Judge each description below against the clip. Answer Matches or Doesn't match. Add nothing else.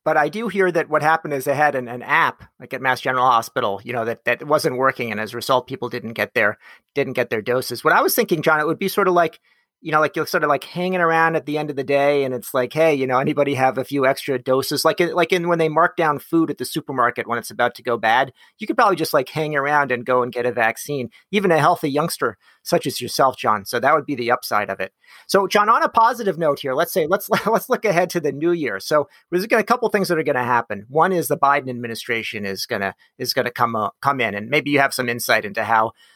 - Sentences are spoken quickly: Matches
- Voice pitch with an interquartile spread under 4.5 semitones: Doesn't match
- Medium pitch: Matches